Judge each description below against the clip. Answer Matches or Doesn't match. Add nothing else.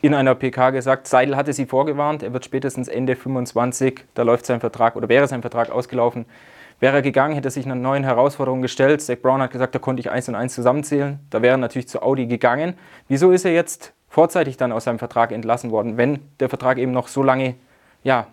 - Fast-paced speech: Matches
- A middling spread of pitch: Doesn't match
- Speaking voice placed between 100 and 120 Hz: Doesn't match